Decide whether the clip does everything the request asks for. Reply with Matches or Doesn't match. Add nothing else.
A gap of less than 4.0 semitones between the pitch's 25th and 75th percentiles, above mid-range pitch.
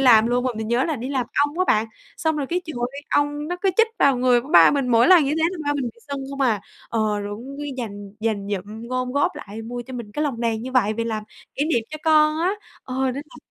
Doesn't match